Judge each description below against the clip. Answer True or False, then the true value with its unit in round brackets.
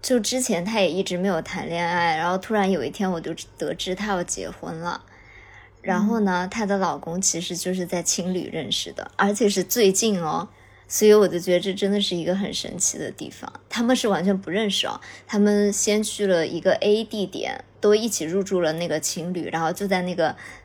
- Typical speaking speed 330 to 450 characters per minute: False (300 characters per minute)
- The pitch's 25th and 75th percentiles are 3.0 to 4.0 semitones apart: True (3.3 semitones)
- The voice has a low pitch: False (185 Hz)